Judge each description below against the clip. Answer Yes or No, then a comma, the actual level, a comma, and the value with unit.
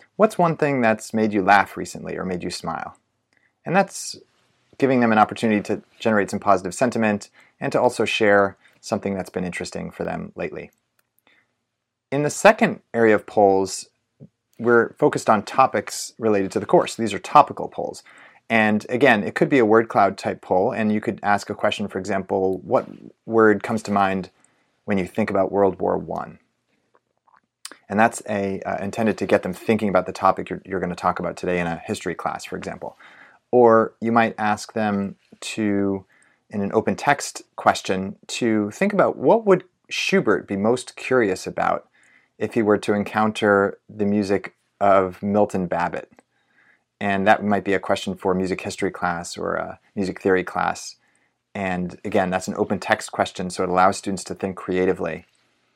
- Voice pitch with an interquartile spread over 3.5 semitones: No, average, 2.7 semitones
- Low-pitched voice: Yes, low, 100 Hz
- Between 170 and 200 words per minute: Yes, average, 180 wpm